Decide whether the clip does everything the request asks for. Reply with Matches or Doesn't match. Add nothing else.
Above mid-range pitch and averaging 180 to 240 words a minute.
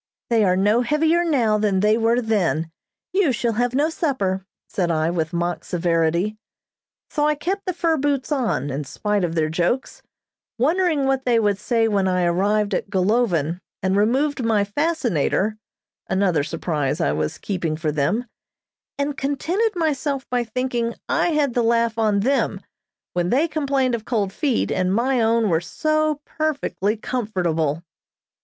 Doesn't match